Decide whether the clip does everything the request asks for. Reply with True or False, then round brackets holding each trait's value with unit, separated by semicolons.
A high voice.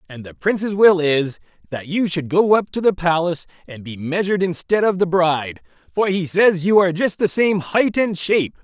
False (175 Hz)